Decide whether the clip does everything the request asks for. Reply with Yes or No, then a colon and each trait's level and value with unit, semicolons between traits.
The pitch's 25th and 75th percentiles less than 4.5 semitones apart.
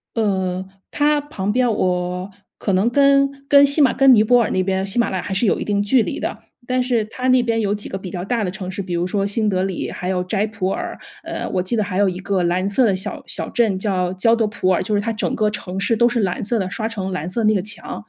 Yes: average, 3.7 semitones